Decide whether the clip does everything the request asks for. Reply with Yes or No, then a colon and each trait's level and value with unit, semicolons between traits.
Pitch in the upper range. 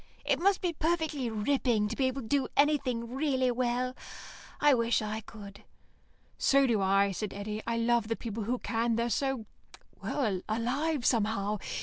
Yes: high, 235 Hz